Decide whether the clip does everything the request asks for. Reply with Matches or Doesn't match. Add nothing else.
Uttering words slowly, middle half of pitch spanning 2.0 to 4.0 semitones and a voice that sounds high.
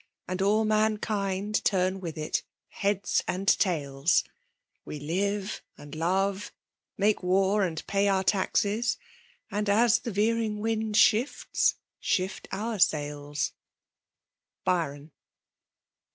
Matches